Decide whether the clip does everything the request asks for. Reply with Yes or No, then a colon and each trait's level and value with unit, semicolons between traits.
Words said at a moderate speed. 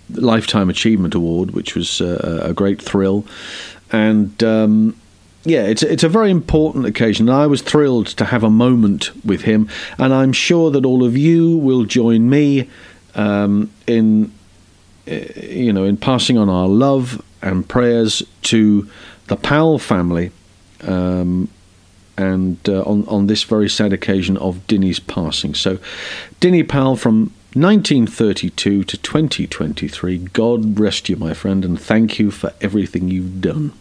Yes: average, 155 wpm